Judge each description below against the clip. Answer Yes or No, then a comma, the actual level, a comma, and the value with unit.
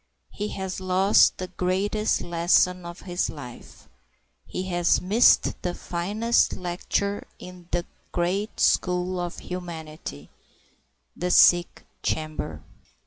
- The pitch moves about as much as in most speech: No, narrow, 1.5 semitones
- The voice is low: No, medium, 180 Hz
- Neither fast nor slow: No, slow, 110 wpm